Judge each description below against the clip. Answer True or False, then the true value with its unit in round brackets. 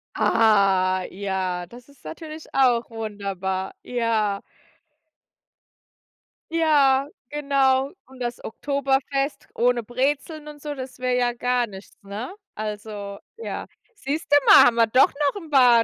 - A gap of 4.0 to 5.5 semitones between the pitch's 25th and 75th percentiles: True (4.9 semitones)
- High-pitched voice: True (245 Hz)